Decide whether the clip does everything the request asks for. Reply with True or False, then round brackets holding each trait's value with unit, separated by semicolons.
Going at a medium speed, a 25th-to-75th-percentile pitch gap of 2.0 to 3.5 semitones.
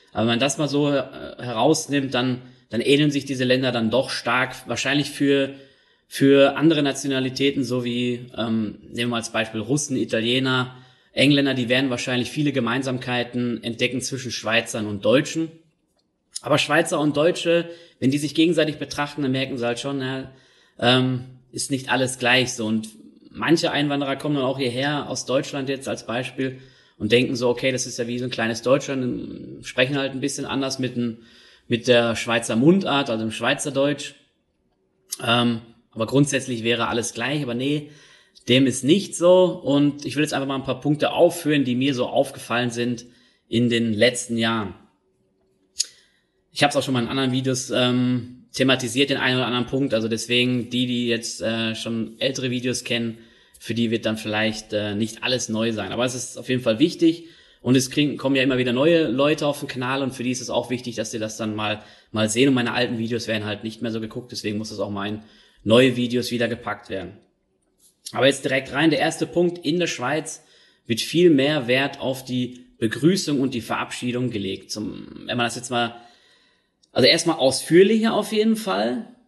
False (195 wpm; 2.9 semitones)